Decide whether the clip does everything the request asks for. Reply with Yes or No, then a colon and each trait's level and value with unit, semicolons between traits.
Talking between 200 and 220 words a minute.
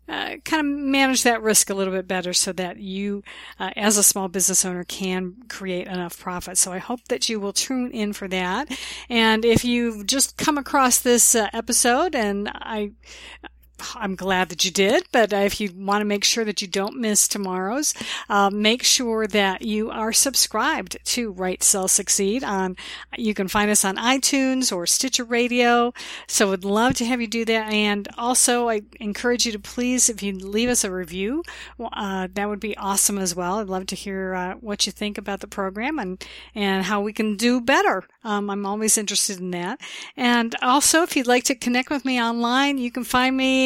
Yes: fast, 205 wpm